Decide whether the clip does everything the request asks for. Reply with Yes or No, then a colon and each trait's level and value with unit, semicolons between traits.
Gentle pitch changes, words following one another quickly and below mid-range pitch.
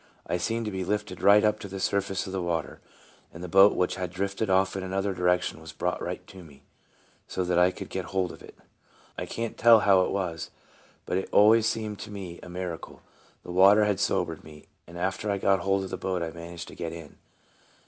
Yes: narrow, 2.3 semitones; fast, 230 wpm; very low, 95 Hz